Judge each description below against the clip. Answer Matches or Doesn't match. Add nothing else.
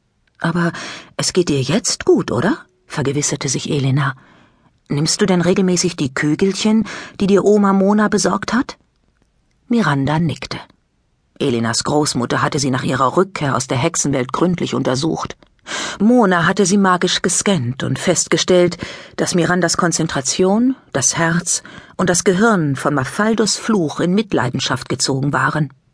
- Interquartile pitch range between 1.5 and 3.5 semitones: Doesn't match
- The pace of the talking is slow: Doesn't match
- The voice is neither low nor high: Matches